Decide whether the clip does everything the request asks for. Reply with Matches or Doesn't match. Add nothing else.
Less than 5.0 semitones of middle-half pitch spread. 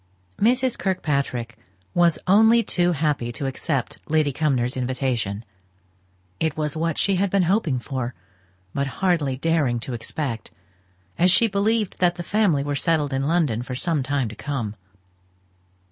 Doesn't match